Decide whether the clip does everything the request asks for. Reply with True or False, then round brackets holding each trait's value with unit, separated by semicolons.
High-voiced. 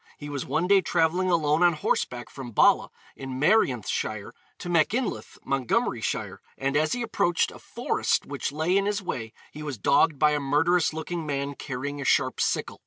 False (150 Hz)